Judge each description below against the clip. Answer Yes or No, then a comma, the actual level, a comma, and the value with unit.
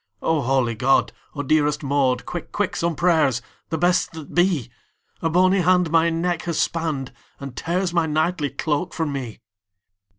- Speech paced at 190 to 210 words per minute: No, average, 165 wpm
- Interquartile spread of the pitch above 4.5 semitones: No, average, 3.7 semitones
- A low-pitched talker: No, medium, 160 Hz